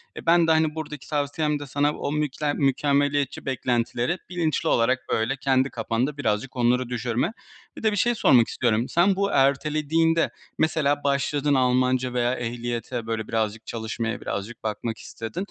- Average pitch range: Yes, average, 4.1 semitones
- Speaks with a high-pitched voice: No, low, 135 Hz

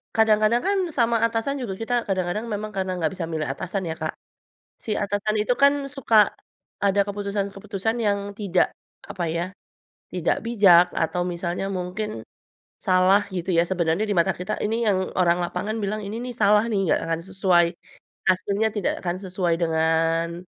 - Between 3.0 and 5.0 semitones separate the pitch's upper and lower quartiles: Yes, average, 3.4 semitones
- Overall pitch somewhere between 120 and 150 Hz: No, high, 195 Hz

